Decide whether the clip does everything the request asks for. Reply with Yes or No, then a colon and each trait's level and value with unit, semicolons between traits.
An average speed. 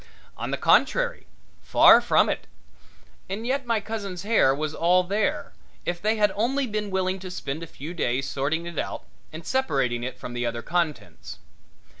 Yes: average, 175 wpm